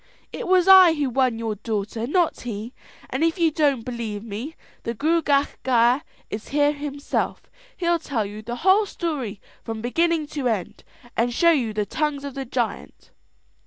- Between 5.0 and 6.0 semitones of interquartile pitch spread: Yes, wide, 5.6 semitones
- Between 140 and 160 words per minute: No, average, 170 wpm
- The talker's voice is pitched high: Yes, very high, 265 Hz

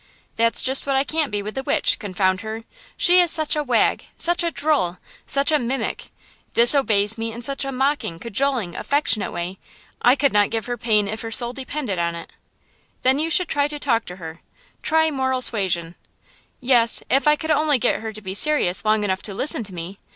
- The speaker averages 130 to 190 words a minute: No, average, 200 wpm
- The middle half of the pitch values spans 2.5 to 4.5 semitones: No, wide, 5.6 semitones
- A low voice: No, high, 240 Hz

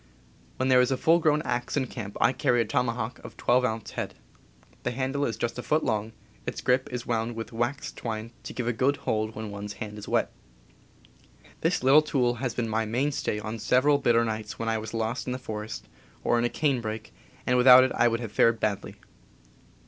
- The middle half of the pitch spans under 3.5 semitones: Yes, narrow, 2.6 semitones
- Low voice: Yes, low, 120 Hz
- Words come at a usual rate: No, fast, 215 wpm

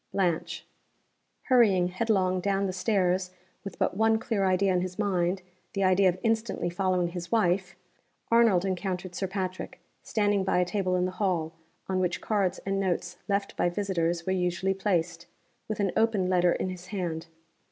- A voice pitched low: No, medium, 185 Hz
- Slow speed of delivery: No, average, 170 wpm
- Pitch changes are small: Yes, narrow, 1.9 semitones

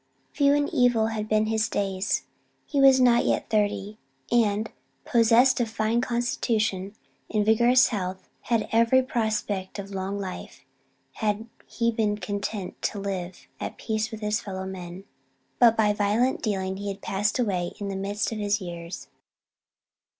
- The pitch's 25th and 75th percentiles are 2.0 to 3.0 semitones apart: Yes, average, 2.7 semitones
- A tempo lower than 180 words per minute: Yes, average, 155 wpm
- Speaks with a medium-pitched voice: No, high, 215 Hz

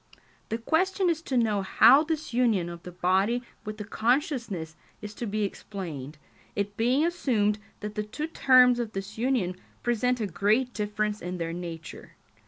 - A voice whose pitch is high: Yes, high, 215 Hz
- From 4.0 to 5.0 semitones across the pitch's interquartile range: Yes, average, 4.4 semitones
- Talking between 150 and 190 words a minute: Yes, average, 170 wpm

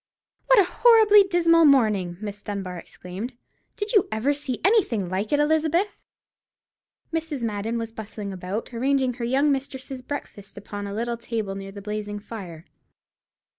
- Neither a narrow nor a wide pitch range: No, wide, 6.3 semitones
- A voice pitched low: No, high, 235 Hz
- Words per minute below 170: Yes, average, 150 wpm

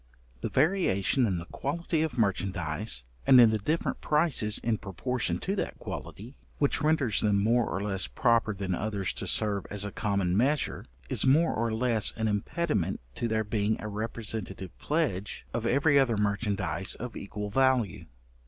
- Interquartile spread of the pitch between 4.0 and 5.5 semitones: Yes, average, 4.7 semitones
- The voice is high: No, low, 110 Hz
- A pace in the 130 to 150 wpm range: No, average, 170 wpm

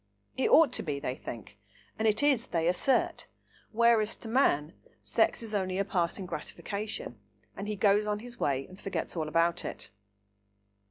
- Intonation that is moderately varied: Yes, average, 4.9 semitones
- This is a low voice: No, high, 200 Hz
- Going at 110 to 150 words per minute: No, average, 170 wpm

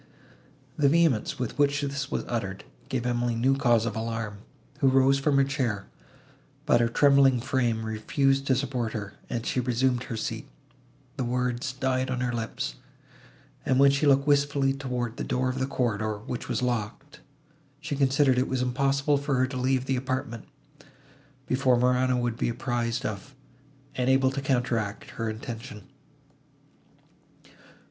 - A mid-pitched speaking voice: No, low, 130 Hz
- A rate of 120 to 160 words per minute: Yes, average, 155 wpm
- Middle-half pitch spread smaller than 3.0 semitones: Yes, narrow, 2.6 semitones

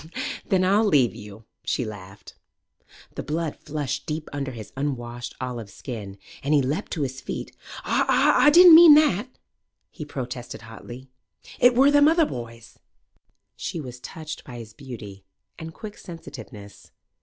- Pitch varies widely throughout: Yes, wide, 6.2 semitones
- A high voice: No, low, 135 Hz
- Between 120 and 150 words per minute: Yes, average, 145 wpm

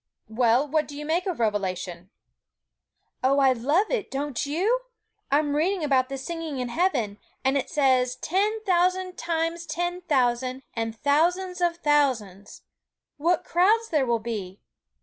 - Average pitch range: No, wide, 5.8 semitones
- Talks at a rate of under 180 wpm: Yes, average, 150 wpm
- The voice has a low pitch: No, very high, 290 Hz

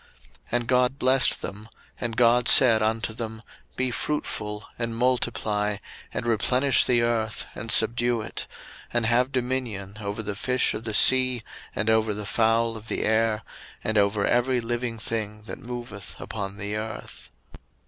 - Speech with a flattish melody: Yes, narrow, 2.2 semitones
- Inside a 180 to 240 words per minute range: No, average, 160 wpm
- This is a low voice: Yes, low, 115 Hz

